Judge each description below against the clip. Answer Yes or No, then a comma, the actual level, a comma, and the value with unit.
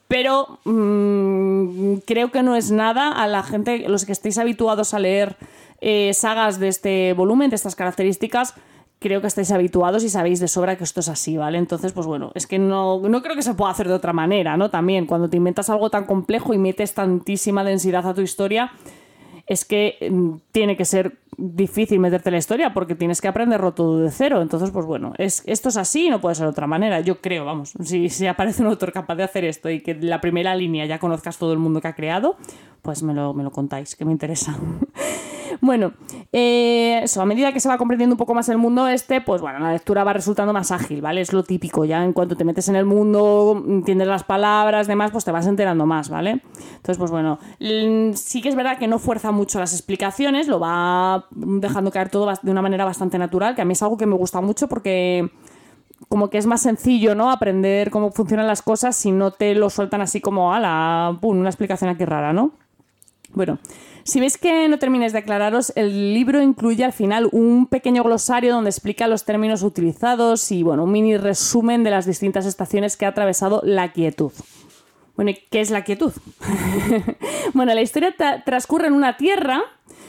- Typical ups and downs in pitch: Yes, average, 3.9 semitones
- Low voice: No, high, 200 Hz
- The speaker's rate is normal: No, fast, 215 wpm